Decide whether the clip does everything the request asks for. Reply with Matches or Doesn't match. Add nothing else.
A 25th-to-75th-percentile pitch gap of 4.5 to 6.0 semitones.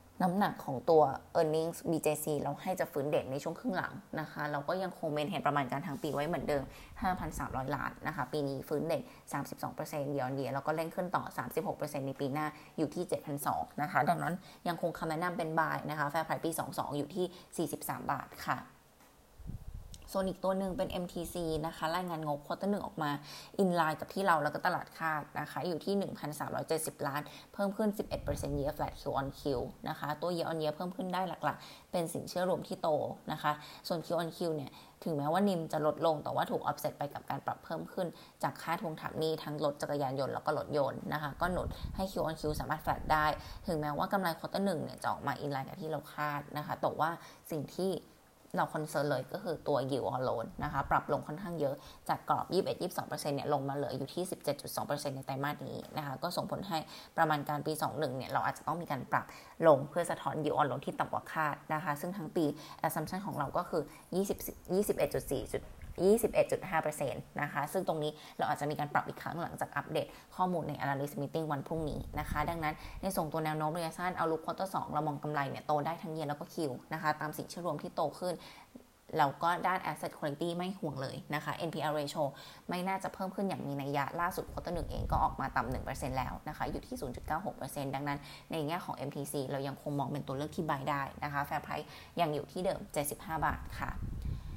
Doesn't match